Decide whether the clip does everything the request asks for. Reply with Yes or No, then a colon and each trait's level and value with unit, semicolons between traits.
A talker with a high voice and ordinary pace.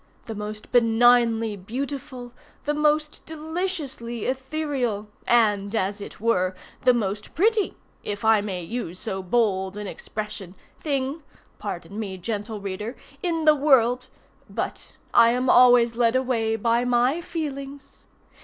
No: high, 235 Hz; slow, 125 wpm